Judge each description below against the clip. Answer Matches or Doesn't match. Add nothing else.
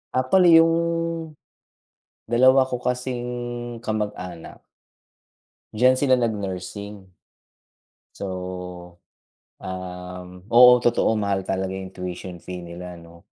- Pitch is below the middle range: Matches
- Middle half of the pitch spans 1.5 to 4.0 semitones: Doesn't match